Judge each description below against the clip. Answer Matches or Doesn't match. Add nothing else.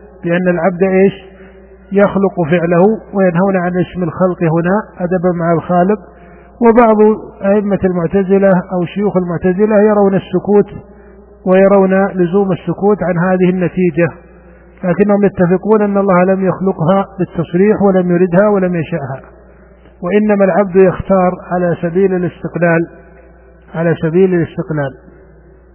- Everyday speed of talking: Matches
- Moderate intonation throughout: Doesn't match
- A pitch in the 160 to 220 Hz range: Matches